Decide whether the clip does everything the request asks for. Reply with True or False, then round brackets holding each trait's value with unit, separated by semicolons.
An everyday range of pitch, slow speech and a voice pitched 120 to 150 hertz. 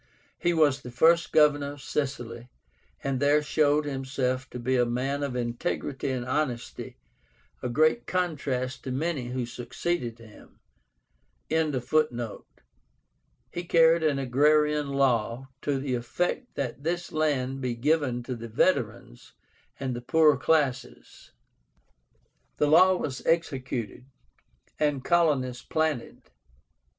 True (3.7 semitones; 120 wpm; 135 Hz)